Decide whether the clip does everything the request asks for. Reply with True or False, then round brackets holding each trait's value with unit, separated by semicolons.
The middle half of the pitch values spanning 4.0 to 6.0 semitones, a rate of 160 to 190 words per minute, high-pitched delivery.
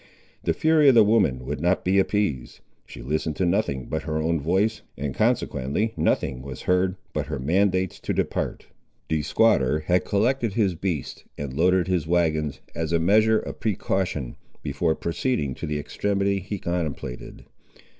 False (5.1 semitones; 165 wpm; 85 Hz)